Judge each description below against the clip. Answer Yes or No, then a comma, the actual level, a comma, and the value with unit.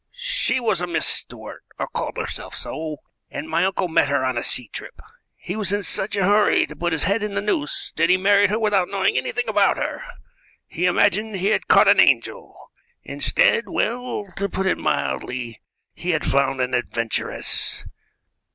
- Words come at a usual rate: Yes, average, 190 wpm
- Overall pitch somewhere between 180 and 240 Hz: Yes, high, 190 Hz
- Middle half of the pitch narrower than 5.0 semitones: No, wide, 5.6 semitones